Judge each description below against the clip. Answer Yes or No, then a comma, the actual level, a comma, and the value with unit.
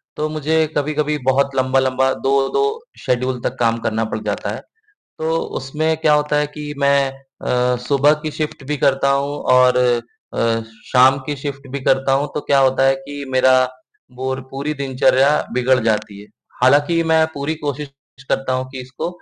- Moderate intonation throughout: No, narrow, 2.3 semitones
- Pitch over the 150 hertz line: No, low, 135 Hz